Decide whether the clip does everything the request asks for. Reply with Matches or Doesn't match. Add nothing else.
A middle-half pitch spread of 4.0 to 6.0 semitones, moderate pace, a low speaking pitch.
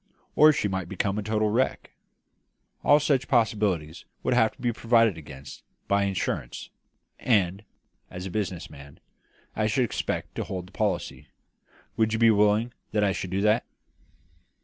Doesn't match